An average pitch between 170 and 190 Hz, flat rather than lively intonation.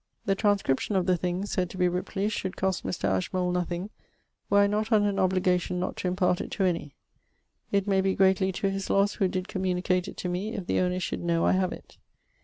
Yes: medium, 185 Hz; narrow, 1.6 semitones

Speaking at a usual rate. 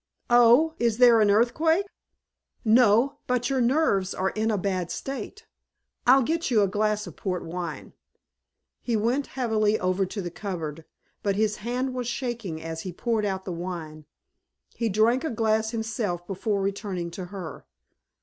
Yes: average, 160 wpm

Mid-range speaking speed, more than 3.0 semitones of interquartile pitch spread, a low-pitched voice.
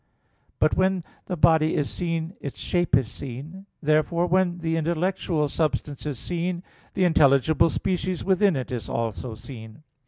No: average, 150 wpm; average, 4.1 semitones; medium, 160 Hz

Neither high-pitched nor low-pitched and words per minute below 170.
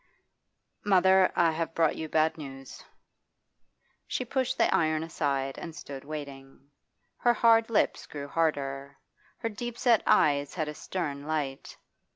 Yes: medium, 155 Hz; average, 140 wpm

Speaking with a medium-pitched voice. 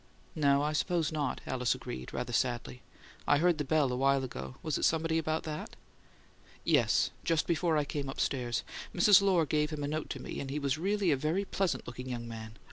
Yes: medium, 150 Hz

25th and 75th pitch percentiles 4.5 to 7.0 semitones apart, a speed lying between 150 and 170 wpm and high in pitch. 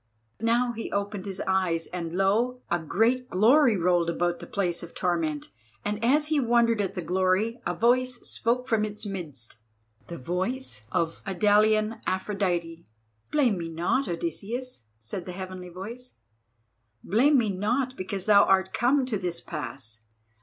Yes: average, 5.2 semitones; average, 155 wpm; high, 195 Hz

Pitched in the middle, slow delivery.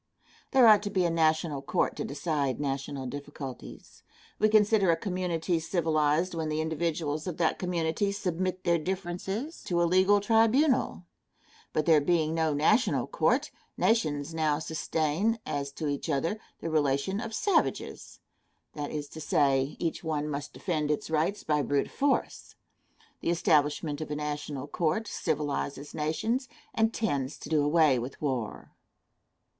No: medium, 160 Hz; average, 150 wpm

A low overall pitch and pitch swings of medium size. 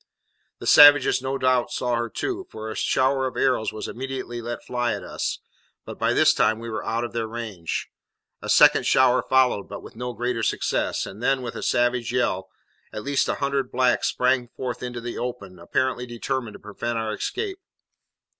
No: low, 120 Hz; narrow, 2.2 semitones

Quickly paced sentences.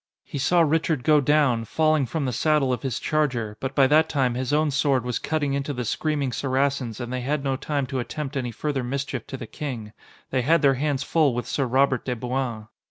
Yes: fast, 225 wpm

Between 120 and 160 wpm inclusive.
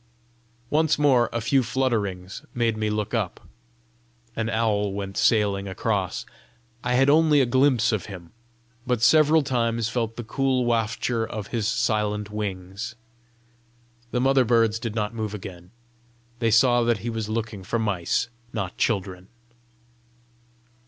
Yes: average, 140 wpm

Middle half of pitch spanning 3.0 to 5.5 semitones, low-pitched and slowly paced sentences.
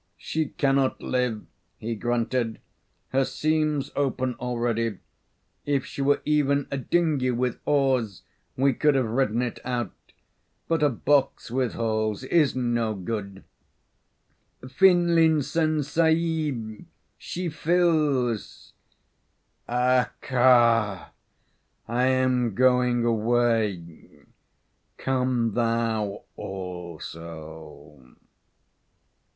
Yes: average, 3.9 semitones; low, 125 Hz; slow, 90 wpm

